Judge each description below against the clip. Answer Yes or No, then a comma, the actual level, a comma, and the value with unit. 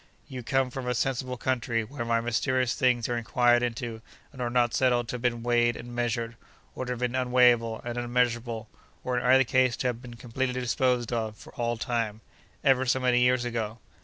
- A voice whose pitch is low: Yes, low, 120 Hz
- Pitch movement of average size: No, narrow, 1.2 semitones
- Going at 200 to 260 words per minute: No, average, 190 wpm